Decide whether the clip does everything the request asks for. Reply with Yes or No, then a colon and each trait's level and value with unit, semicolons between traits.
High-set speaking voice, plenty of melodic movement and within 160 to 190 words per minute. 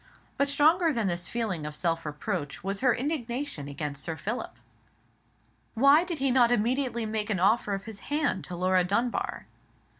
Yes: high, 220 Hz; wide, 6.8 semitones; average, 170 wpm